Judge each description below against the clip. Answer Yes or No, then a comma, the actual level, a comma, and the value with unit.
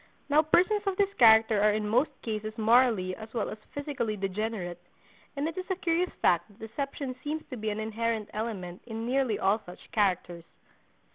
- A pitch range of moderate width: Yes, average, 4.9 semitones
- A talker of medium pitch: No, high, 220 Hz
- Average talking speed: Yes, average, 185 wpm